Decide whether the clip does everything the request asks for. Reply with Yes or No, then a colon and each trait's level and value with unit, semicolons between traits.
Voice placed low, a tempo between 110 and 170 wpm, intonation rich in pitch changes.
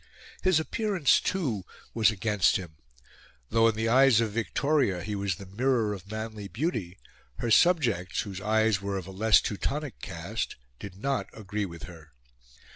No: low, 110 Hz; average, 160 wpm; average, 4.0 semitones